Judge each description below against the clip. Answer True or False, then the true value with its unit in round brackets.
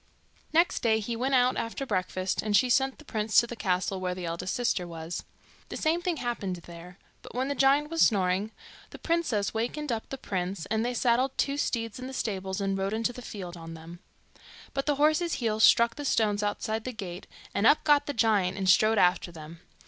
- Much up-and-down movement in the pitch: True (5.7 semitones)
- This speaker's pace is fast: True (215 wpm)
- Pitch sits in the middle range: False (220 Hz)